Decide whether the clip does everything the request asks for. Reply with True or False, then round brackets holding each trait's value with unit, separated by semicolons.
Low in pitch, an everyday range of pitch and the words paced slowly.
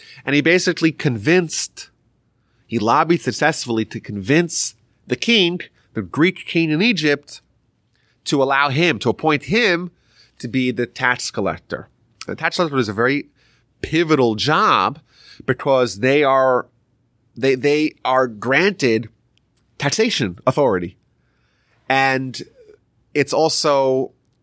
True (130 Hz; 4.8 semitones; 115 wpm)